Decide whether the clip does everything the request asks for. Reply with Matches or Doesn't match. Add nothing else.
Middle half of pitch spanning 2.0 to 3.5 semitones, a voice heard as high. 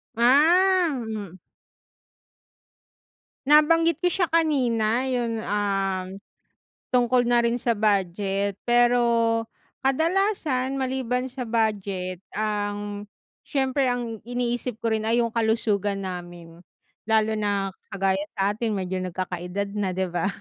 Doesn't match